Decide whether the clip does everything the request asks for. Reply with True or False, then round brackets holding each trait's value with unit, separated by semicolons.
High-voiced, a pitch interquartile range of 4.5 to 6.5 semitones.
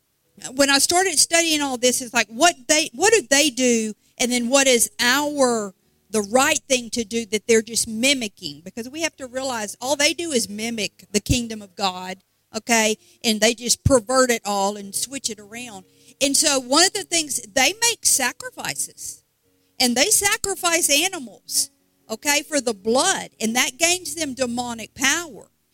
True (255 Hz; 4.8 semitones)